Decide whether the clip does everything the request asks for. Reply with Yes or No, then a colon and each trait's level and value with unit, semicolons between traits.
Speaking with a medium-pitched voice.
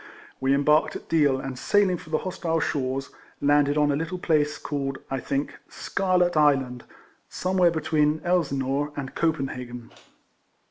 Yes: medium, 145 Hz